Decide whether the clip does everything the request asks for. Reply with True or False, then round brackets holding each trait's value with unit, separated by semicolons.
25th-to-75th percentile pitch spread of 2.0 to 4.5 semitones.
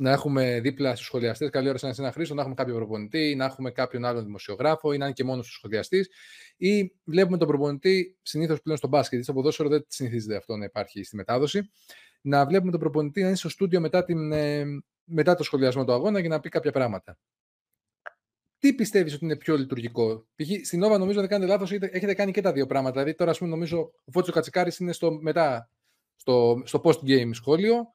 False (5.6 semitones)